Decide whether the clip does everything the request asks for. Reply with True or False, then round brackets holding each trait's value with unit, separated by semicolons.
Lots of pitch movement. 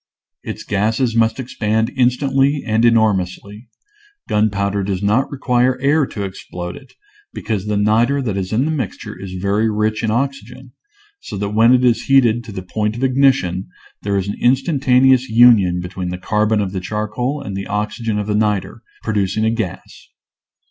False (3.8 semitones)